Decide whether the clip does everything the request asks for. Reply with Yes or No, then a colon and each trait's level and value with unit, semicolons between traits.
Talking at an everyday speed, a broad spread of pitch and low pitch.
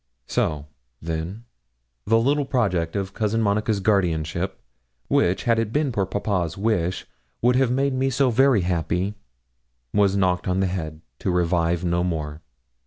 No: average, 155 wpm; average, 4.8 semitones; very low, 95 Hz